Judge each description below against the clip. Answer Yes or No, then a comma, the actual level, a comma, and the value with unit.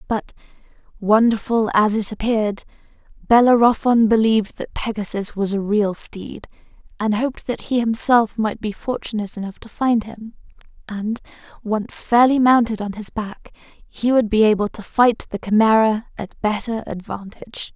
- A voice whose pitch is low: No, high, 220 Hz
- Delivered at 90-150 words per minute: Yes, average, 145 wpm